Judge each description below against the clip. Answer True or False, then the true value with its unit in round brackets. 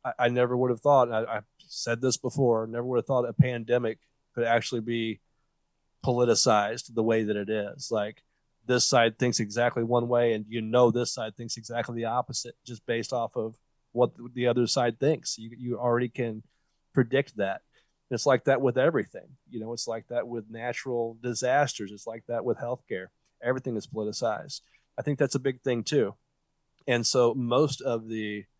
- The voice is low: True (120 Hz)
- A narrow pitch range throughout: True (1.8 semitones)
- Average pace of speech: True (185 wpm)